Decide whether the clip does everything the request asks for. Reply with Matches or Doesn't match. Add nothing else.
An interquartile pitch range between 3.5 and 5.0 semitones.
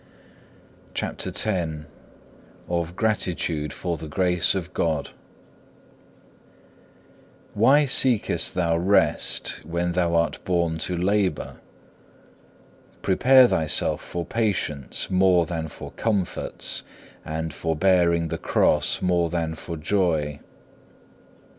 Doesn't match